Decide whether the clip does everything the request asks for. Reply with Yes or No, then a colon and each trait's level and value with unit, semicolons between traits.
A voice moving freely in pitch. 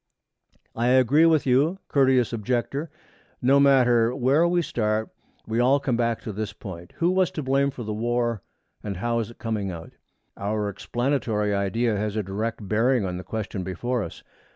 No: average, 3.9 semitones